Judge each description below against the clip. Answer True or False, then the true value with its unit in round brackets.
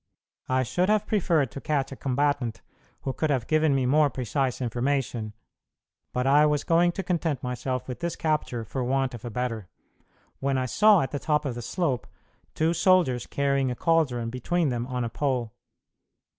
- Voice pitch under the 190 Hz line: True (135 Hz)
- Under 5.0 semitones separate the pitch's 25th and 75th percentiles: True (3.9 semitones)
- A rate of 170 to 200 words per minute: True (185 wpm)